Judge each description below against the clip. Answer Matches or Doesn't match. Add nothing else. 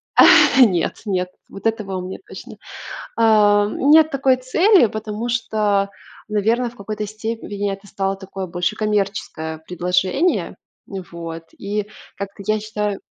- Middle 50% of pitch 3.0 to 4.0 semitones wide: Doesn't match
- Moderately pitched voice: Doesn't match